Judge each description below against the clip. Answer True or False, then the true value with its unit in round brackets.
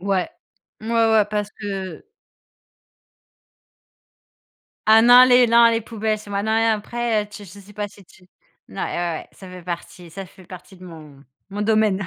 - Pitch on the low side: False (205 Hz)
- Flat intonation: False (3.2 semitones)